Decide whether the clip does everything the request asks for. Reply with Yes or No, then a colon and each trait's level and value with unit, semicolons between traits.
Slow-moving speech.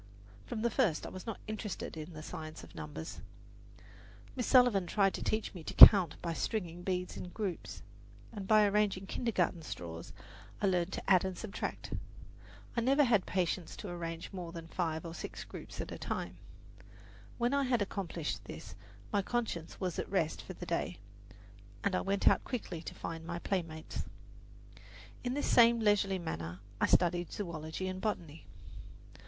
No: average, 170 wpm